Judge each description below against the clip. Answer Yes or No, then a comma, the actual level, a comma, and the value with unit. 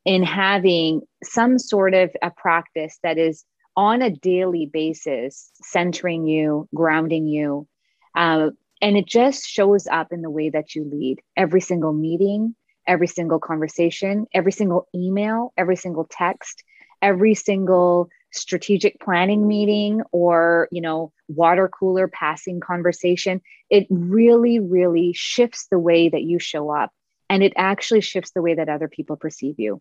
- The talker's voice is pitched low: No, medium, 180 Hz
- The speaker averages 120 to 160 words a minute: Yes, average, 150 wpm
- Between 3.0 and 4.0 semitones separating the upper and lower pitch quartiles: Yes, average, 3.5 semitones